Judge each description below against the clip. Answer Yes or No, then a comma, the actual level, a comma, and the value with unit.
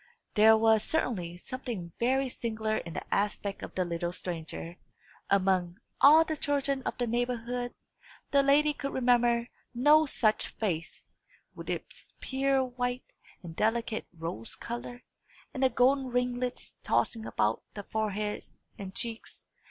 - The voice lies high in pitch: Yes, high, 235 Hz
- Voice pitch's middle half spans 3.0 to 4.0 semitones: No, average, 4.4 semitones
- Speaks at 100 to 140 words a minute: Yes, slow, 135 wpm